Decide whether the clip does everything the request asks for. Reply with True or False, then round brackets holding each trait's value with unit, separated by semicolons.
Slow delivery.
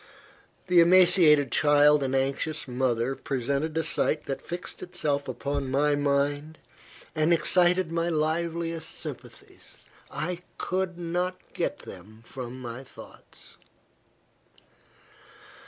True (105 wpm)